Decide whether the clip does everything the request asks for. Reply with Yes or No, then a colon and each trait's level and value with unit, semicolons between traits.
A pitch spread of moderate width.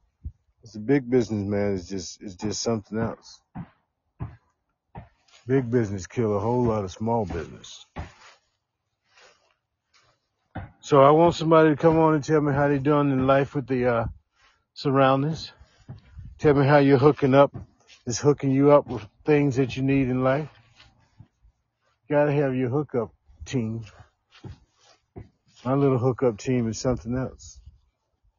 Yes: average, 5.0 semitones